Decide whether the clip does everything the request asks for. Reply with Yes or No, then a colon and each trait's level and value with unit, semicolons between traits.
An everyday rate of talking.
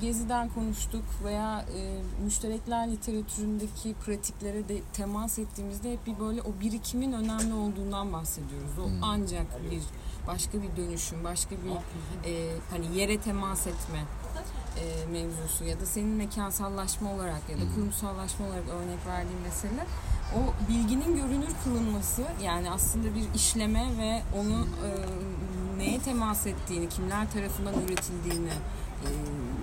Yes: average, 130 wpm